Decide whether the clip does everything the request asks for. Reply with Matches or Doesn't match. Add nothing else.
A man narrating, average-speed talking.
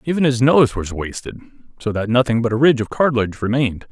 Doesn't match